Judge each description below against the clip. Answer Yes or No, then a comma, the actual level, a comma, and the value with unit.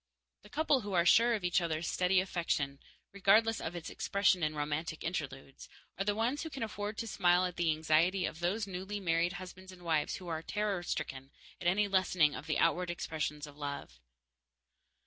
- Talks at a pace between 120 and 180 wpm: No, average, 190 wpm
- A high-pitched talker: No, medium, 180 Hz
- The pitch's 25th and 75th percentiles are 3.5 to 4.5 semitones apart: Yes, average, 3.9 semitones